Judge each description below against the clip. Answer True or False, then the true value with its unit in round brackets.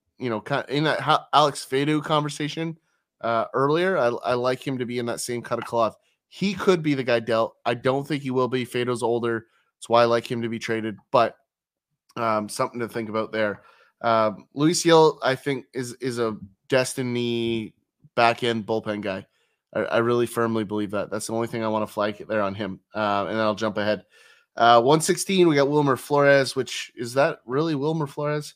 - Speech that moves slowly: False (205 wpm)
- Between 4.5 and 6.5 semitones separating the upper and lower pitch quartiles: False (4.1 semitones)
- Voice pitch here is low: True (120 Hz)